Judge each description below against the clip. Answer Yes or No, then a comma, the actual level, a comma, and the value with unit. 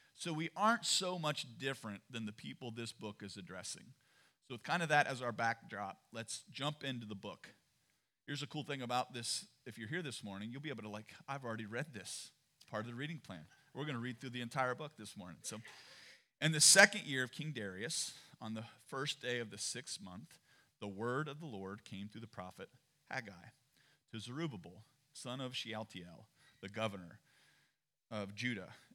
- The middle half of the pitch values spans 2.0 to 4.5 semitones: No, average, 5.0 semitones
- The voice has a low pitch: Yes, low, 125 Hz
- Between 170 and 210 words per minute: Yes, average, 200 wpm